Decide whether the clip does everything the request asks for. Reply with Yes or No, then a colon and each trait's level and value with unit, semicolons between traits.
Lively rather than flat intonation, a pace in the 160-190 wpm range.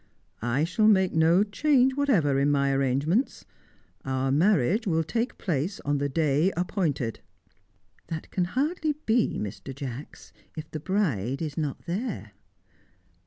No: wide, 6.9 semitones; slow, 135 wpm